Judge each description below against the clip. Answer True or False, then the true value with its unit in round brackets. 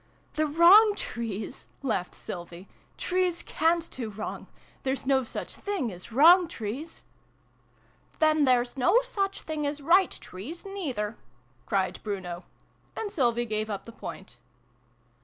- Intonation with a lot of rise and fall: True (8.2 semitones)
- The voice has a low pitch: False (265 Hz)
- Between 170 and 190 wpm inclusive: False (155 wpm)